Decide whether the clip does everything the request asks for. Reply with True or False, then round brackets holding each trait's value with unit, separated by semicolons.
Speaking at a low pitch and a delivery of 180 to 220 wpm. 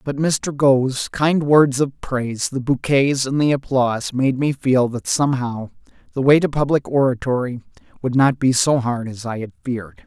True (130 Hz; 185 wpm)